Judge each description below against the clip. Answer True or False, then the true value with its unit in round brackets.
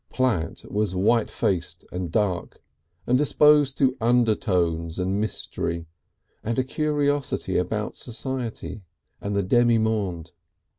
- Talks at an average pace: False (115 wpm)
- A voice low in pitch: True (110 Hz)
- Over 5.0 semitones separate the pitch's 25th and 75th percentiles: True (5.6 semitones)